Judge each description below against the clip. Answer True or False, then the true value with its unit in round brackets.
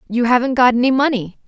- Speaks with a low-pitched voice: False (245 Hz)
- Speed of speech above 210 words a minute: False (205 wpm)